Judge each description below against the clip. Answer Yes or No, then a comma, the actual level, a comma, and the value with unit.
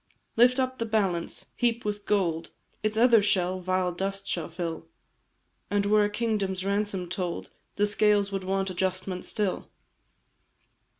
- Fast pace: No, average, 140 wpm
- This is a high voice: Yes, high, 195 Hz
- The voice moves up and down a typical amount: No, narrow, 2.2 semitones